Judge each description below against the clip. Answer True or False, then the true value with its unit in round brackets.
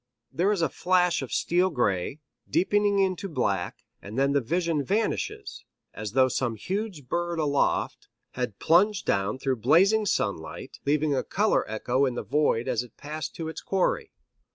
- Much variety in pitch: True (6.7 semitones)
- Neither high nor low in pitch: True (150 Hz)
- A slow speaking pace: False (165 wpm)